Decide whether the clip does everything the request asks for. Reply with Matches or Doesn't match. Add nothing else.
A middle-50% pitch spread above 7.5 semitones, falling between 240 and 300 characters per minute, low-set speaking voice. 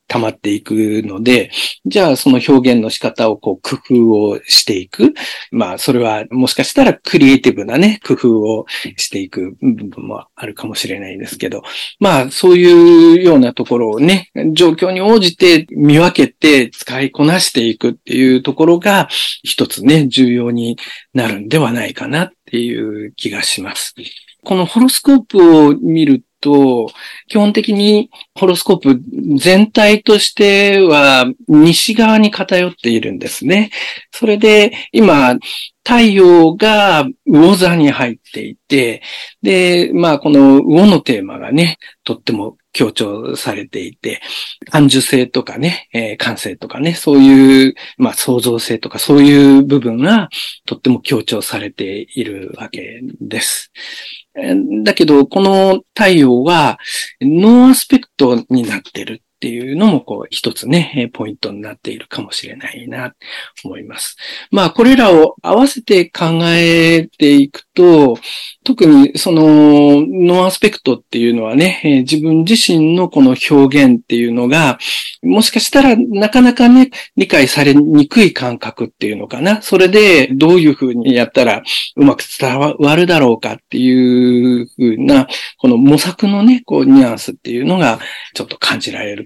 Doesn't match